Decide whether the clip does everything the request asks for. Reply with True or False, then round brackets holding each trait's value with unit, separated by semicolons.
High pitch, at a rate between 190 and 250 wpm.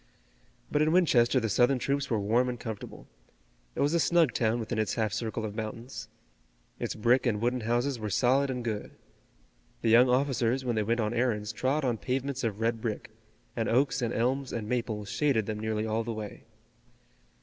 False (120 Hz; 195 wpm)